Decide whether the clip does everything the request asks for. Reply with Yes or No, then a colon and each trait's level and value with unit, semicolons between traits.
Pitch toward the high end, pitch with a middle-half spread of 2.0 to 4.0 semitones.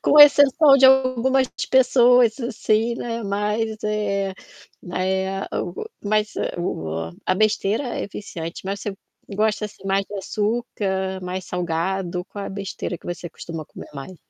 Yes: high, 200 Hz; average, 3.6 semitones